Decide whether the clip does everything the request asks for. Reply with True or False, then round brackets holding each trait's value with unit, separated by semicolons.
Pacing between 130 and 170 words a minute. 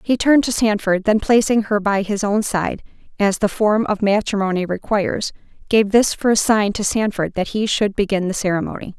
False (195 wpm)